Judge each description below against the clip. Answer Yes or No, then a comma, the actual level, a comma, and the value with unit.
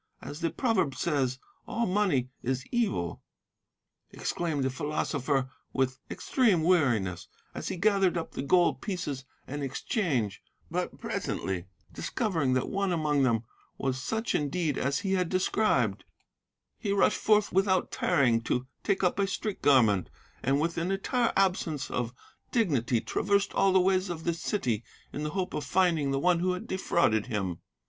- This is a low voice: No, medium, 160 Hz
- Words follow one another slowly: No, average, 155 wpm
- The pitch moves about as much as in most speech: No, wide, 6.5 semitones